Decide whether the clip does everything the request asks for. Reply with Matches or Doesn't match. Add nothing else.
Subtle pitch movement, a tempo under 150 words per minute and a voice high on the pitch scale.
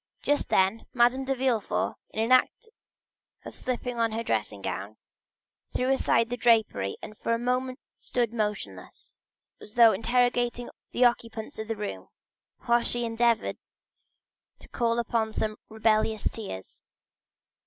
Matches